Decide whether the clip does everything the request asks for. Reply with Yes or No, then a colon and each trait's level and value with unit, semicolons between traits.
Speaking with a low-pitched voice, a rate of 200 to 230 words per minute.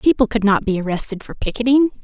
No: high, 225 Hz; fast, 205 wpm